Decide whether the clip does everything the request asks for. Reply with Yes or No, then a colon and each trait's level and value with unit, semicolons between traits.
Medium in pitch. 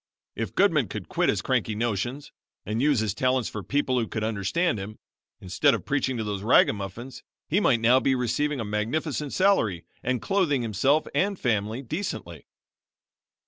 No: low, 120 Hz